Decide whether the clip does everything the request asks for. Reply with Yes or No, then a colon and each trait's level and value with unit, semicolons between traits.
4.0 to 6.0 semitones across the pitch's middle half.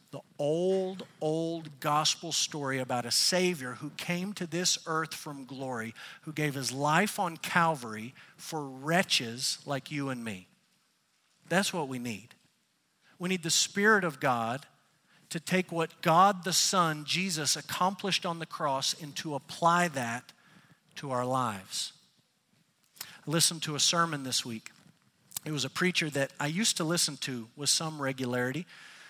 Yes: average, 4.5 semitones